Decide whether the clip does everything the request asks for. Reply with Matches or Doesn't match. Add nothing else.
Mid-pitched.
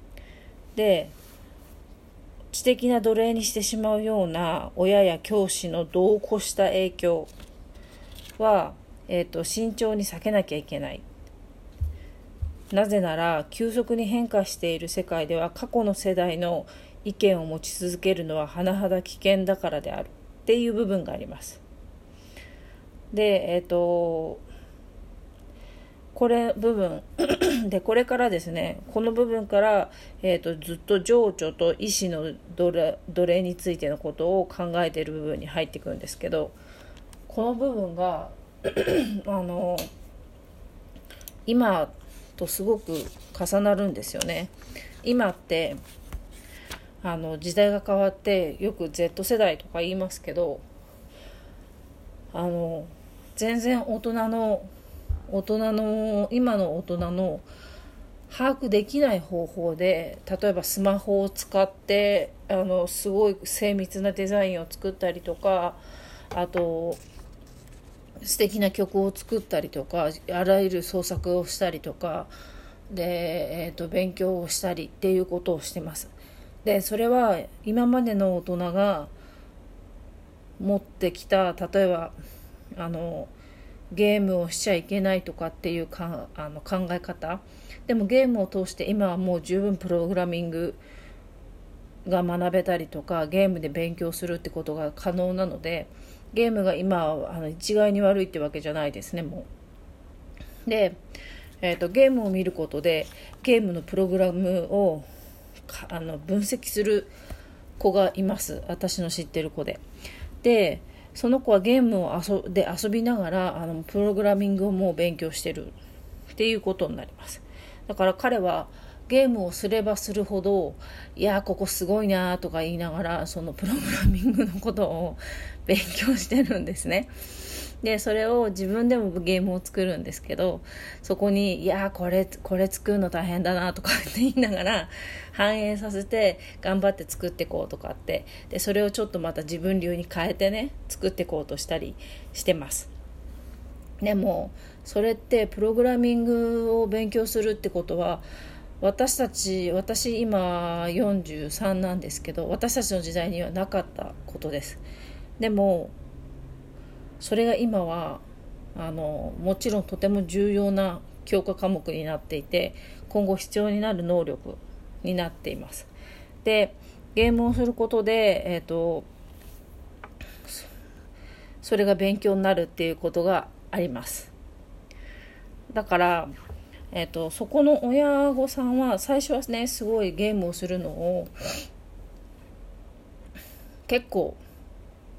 Matches